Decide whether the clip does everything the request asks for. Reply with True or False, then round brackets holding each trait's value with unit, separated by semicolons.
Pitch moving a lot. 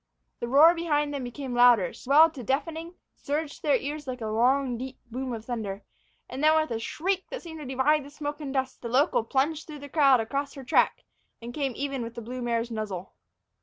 False (3.7 semitones)